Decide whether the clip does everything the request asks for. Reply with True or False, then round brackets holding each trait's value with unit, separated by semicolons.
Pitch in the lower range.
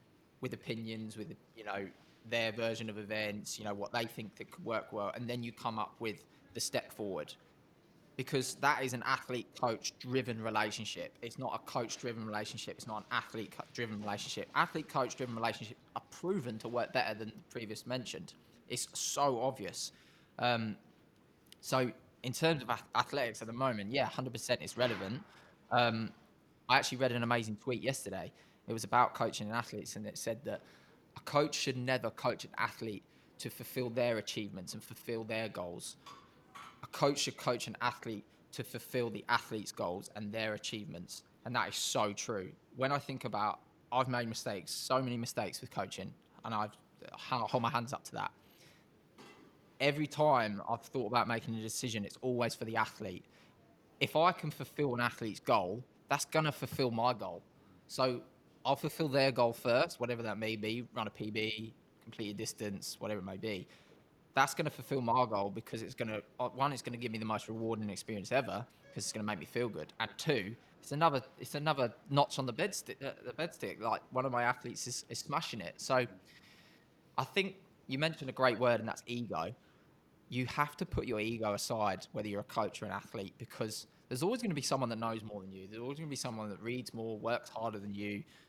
True (120 Hz)